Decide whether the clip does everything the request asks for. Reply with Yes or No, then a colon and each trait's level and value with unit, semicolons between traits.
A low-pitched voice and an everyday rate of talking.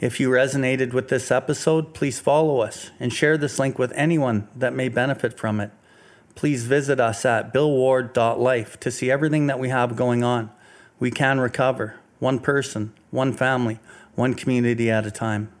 Yes: low, 130 Hz; average, 175 wpm